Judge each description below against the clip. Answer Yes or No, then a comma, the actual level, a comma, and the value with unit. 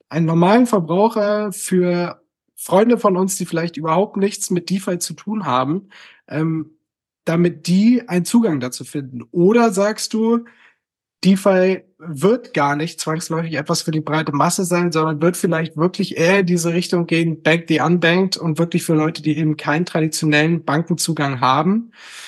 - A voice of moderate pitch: Yes, medium, 170 Hz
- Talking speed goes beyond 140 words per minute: Yes, average, 160 wpm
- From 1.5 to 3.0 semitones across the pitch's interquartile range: No, average, 3.5 semitones